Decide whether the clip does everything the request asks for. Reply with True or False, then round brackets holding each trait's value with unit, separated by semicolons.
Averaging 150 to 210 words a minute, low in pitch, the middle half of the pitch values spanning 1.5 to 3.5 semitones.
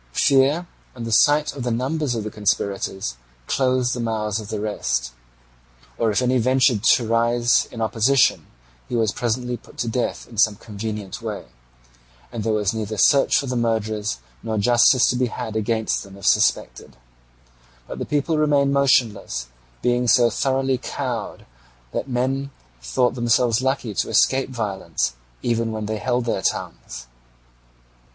True (160 wpm; 115 Hz; 3.0 semitones)